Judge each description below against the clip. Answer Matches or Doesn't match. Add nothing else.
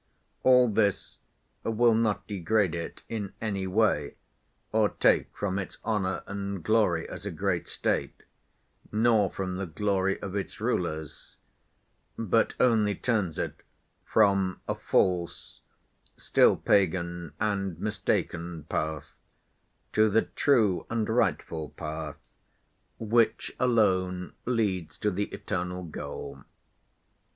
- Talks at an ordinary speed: Doesn't match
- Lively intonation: Doesn't match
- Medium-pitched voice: Doesn't match